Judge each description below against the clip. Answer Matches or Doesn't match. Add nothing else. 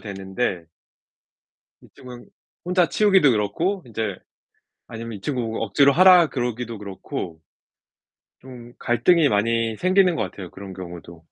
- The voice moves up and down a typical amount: Doesn't match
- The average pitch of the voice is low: Matches